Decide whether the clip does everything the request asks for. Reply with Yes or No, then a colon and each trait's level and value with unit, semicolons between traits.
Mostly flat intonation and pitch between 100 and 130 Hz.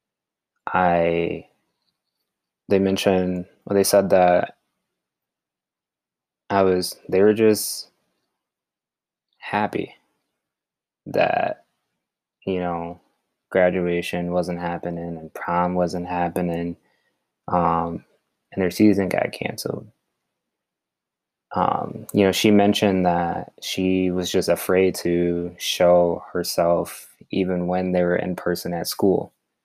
No: narrow, 1.4 semitones; very low, 90 Hz